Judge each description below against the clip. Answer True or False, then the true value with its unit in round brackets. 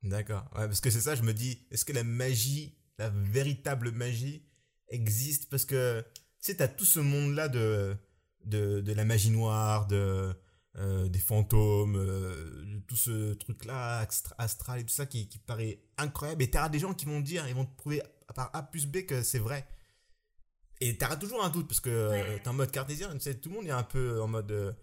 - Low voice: True (120 Hz)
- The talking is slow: False (215 wpm)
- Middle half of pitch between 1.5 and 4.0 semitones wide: False (4.9 semitones)